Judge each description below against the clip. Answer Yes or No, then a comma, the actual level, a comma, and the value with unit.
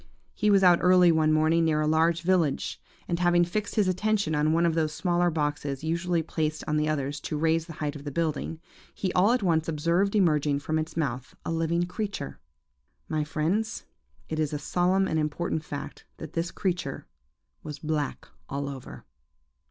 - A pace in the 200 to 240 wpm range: No, average, 185 wpm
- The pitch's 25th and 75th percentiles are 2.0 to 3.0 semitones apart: Yes, narrow, 2.6 semitones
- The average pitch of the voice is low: No, medium, 160 Hz